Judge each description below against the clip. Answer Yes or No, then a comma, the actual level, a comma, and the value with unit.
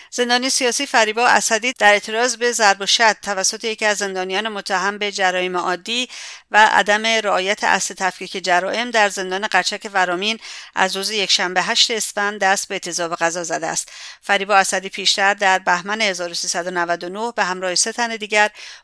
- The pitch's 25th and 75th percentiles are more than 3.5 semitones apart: No, average, 3.0 semitones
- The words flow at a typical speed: Yes, average, 160 wpm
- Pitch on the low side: No, high, 200 Hz